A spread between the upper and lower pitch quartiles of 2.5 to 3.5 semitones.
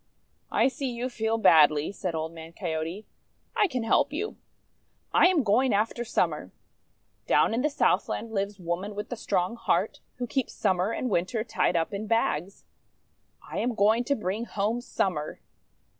No: average, 4.9 semitones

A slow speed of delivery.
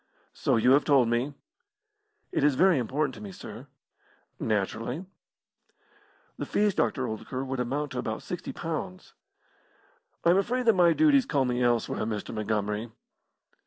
No: average, 150 wpm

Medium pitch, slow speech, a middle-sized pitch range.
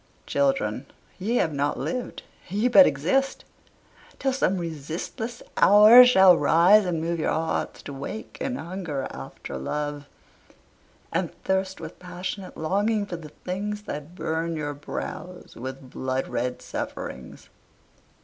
No: medium, 175 Hz; slow, 130 wpm; wide, 6.0 semitones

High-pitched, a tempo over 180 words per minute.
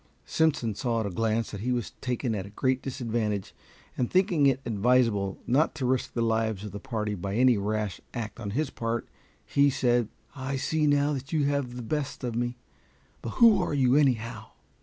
No: low, 120 Hz; average, 200 wpm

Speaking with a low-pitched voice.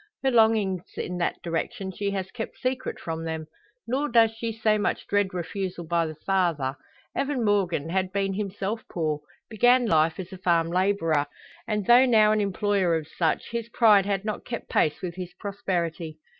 No: high, 195 Hz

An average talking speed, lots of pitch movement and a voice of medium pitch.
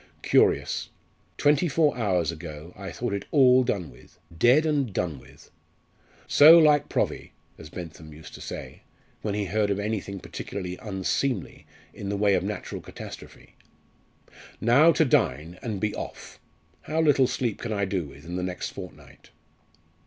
No: average, 160 wpm; wide, 6.5 semitones; low, 100 Hz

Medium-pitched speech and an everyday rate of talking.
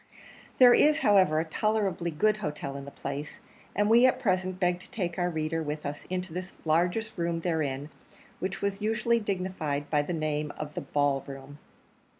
Yes: medium, 175 Hz; average, 180 wpm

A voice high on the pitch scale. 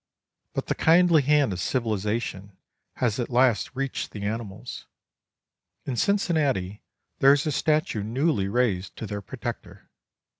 No: low, 120 Hz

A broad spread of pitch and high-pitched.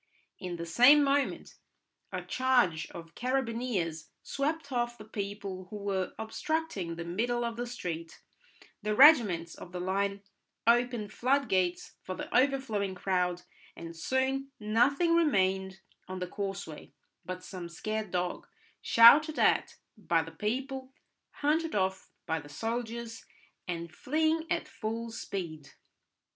Yes: wide, 5.9 semitones; high, 210 Hz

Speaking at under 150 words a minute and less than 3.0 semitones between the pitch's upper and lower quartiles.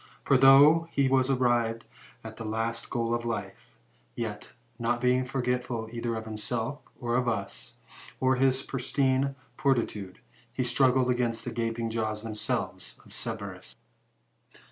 Yes: average, 140 wpm; narrow, 2.4 semitones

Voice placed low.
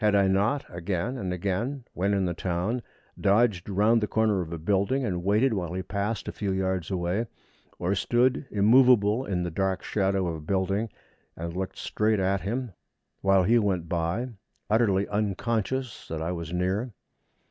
Yes: low, 100 Hz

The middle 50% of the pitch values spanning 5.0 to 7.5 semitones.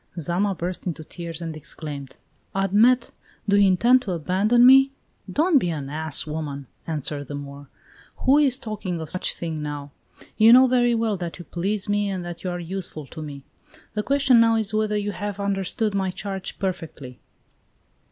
Yes: average, 5.3 semitones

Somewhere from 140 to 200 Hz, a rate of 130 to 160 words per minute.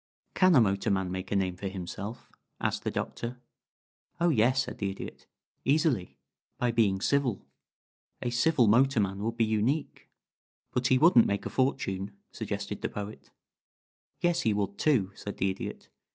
No: low, 110 Hz; average, 155 wpm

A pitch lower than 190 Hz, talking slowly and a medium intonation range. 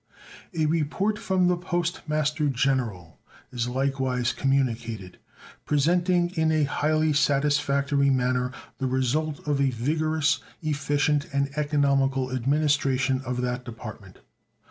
Yes: medium, 140 Hz; slow, 115 wpm; average, 3.1 semitones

